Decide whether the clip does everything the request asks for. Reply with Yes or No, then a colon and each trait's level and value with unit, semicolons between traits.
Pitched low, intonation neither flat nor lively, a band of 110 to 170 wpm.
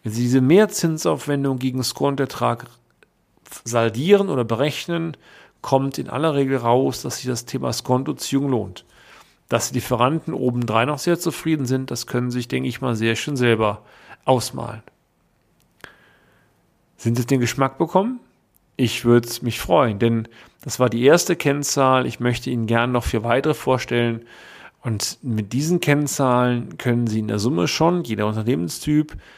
Yes: low, 125 Hz; average, 3.3 semitones; average, 150 wpm